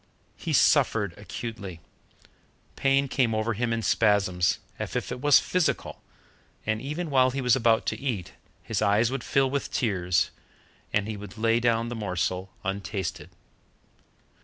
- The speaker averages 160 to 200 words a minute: No, average, 150 wpm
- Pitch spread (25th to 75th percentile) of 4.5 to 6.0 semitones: No, average, 4.1 semitones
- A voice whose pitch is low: Yes, low, 115 Hz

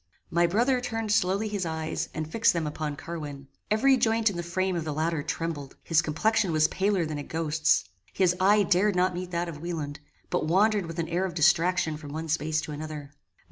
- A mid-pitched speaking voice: Yes, medium, 170 Hz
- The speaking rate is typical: No, fast, 210 wpm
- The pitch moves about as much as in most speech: Yes, average, 3.5 semitones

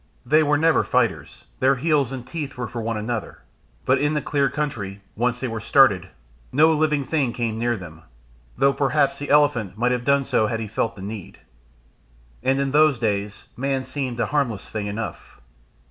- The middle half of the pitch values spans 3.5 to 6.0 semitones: Yes, average, 4.2 semitones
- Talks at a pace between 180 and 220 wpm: Yes, average, 190 wpm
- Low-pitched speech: Yes, low, 125 Hz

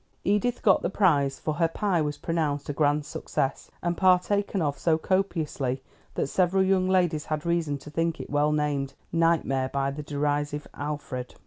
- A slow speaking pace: No, average, 175 wpm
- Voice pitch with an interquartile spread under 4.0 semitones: Yes, average, 3.5 semitones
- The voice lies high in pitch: No, medium, 150 Hz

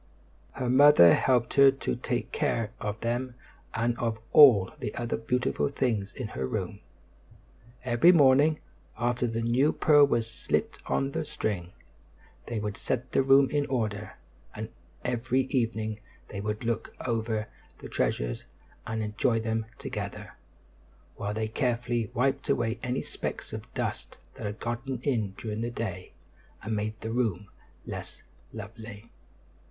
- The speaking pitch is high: No, low, 115 Hz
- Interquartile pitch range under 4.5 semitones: Yes, average, 2.9 semitones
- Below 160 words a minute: Yes, average, 145 wpm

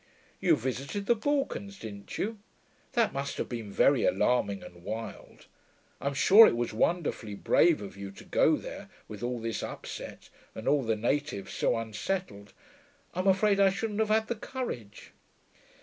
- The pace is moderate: Yes, average, 165 wpm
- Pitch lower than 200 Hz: Yes, low, 135 Hz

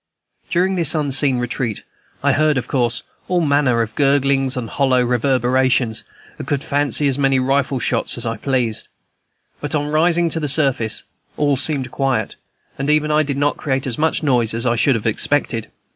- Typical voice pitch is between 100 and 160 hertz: Yes, low, 135 Hz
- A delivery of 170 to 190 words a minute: Yes, average, 180 wpm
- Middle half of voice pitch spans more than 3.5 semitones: No, average, 3.0 semitones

